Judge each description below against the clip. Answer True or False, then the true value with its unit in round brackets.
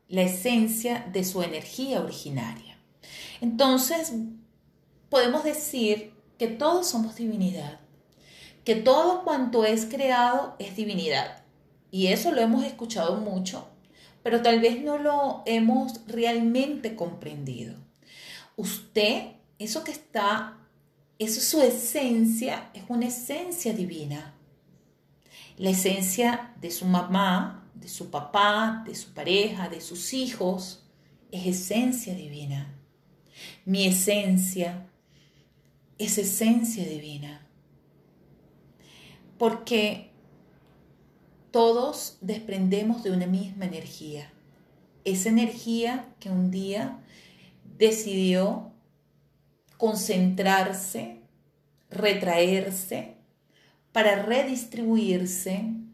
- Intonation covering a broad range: False (4.2 semitones)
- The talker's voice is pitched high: True (210 Hz)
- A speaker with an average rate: False (90 wpm)